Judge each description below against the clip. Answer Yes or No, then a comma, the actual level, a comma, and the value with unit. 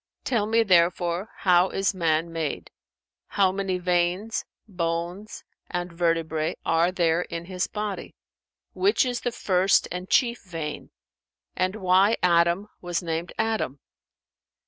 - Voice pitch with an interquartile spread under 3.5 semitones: Yes, average, 2.8 semitones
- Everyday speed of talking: No, slow, 125 wpm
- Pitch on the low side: No, medium, 180 Hz